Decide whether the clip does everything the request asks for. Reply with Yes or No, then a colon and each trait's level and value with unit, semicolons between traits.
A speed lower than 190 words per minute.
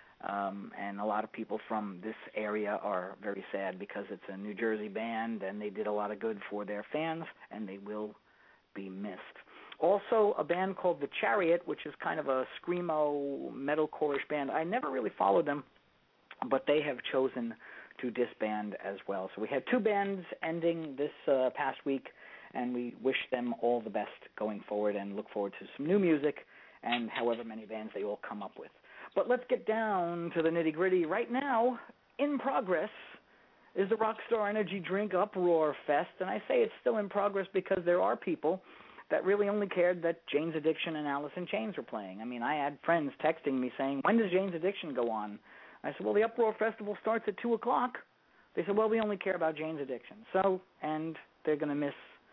No: fast, 205 wpm